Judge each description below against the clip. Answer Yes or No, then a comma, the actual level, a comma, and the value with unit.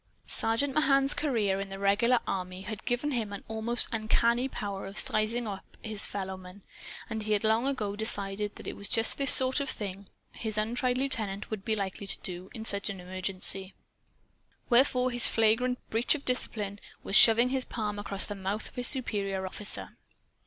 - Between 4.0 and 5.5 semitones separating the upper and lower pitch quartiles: No, average, 3.5 semitones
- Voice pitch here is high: Yes, high, 215 Hz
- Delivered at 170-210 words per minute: Yes, average, 180 wpm